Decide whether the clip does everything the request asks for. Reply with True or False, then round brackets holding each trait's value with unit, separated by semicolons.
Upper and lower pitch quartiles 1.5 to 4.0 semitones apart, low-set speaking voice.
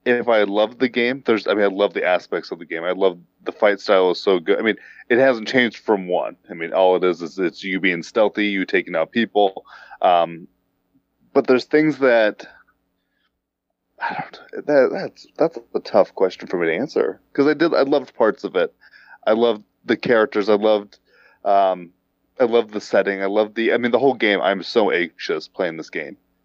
False (4.6 semitones; 105 Hz)